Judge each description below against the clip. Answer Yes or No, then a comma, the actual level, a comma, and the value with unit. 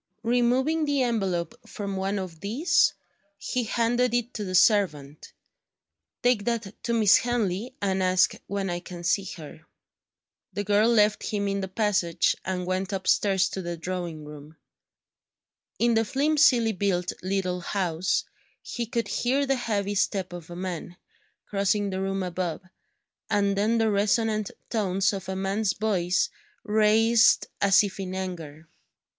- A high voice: Yes, high, 200 Hz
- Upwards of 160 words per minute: No, average, 150 wpm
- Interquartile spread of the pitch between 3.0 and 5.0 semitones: Yes, average, 3.4 semitones